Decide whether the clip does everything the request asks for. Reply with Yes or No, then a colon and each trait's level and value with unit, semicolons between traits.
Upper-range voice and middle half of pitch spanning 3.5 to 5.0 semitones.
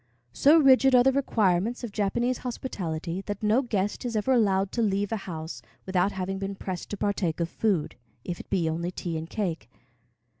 Yes: high, 200 Hz; average, 4.7 semitones